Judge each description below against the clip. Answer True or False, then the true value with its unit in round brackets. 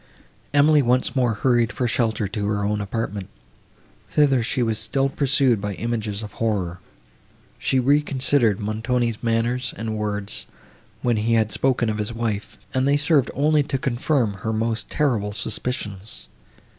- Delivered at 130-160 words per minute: True (150 wpm)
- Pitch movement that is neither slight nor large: True (3.7 semitones)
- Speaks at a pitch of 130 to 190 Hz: False (115 Hz)